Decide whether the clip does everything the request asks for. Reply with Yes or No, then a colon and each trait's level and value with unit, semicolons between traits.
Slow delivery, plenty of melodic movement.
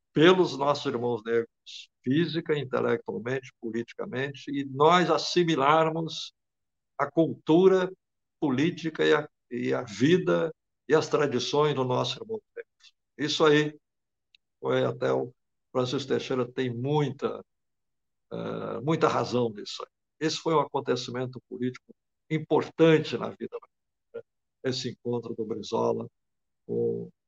No: slow, 110 wpm; average, 4.5 semitones